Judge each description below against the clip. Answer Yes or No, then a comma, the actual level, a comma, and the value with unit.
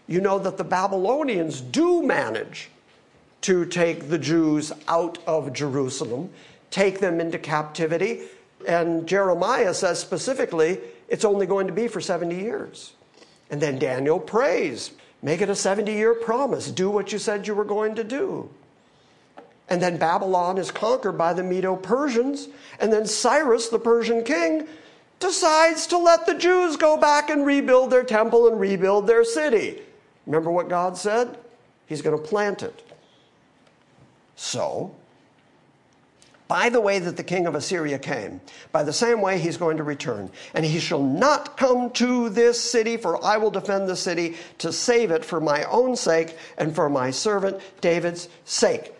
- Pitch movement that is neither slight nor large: No, wide, 5.9 semitones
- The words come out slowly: No, average, 165 wpm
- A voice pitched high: Yes, high, 195 Hz